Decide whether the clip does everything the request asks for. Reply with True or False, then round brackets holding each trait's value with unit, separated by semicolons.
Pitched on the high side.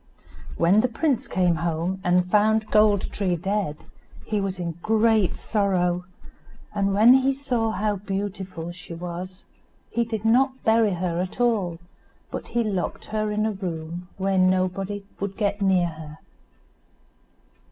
True (195 Hz)